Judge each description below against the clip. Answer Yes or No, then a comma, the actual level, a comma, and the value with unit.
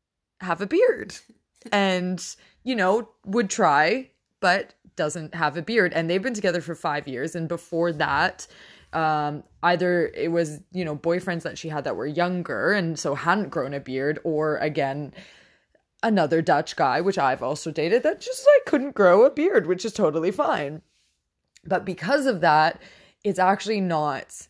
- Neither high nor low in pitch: Yes, medium, 175 Hz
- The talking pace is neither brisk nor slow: Yes, average, 170 wpm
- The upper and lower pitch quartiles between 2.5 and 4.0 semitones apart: No, average, 5.0 semitones